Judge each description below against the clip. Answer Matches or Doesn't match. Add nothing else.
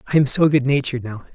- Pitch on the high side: Doesn't match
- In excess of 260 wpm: Doesn't match